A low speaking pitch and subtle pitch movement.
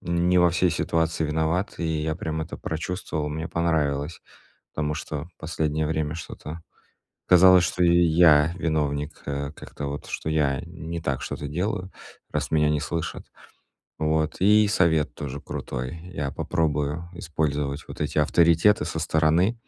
Yes: very low, 80 Hz; narrow, 2.3 semitones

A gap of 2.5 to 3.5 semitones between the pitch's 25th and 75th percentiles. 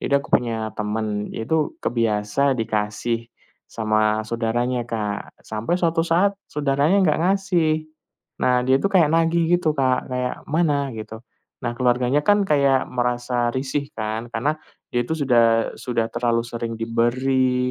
No: average, 4.4 semitones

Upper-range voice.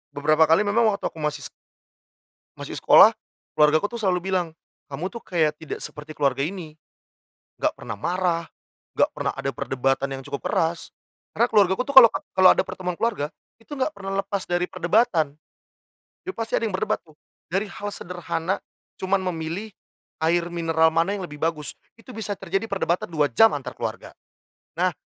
No: medium, 175 Hz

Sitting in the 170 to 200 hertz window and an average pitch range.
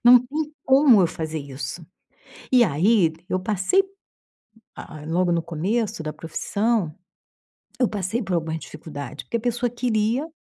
No: high, 190 Hz; wide, 6.8 semitones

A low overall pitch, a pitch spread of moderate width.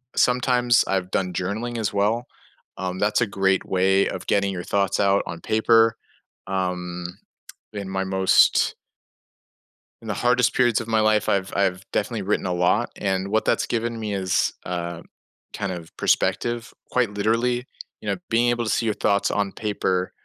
Yes: low, 100 Hz; average, 3.2 semitones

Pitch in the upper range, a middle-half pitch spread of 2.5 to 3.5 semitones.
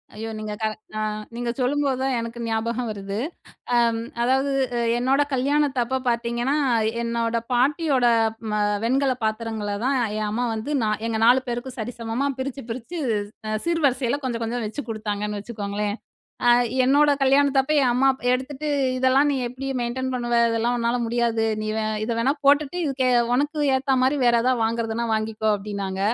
Yes: high, 240 Hz; average, 3.0 semitones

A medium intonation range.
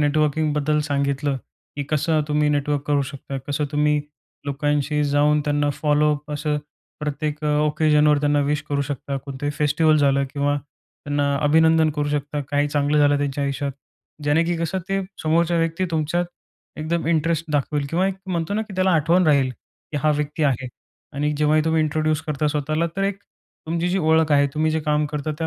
No: narrow, 1.7 semitones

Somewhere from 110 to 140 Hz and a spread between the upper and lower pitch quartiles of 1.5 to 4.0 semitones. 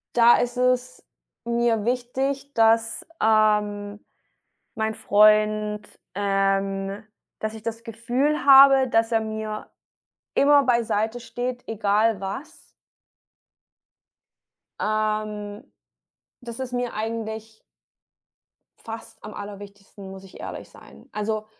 No: high, 220 Hz; narrow, 2.4 semitones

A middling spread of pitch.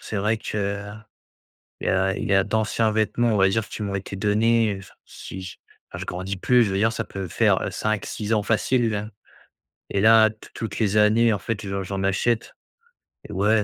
No: narrow, 2.1 semitones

